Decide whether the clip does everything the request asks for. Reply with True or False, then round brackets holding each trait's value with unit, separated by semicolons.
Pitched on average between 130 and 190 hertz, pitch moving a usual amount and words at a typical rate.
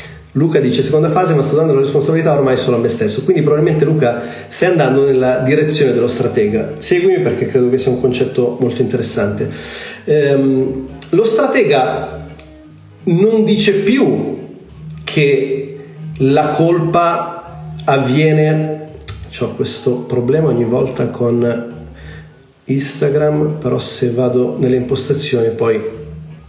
True (135 Hz; 3.7 semitones; 125 wpm)